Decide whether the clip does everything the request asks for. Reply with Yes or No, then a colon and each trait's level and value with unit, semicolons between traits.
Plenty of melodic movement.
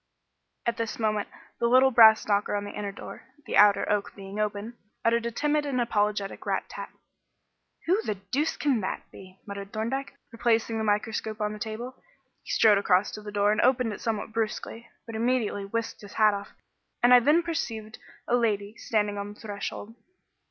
No: narrow, 2.4 semitones